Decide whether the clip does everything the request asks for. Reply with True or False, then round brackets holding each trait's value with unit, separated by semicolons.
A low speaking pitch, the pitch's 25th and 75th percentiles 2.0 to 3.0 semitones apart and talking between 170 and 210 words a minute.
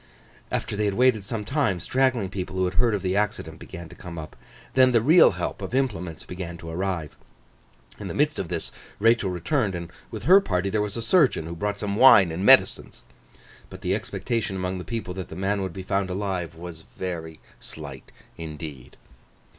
False (95 Hz; 4.1 semitones; 200 wpm)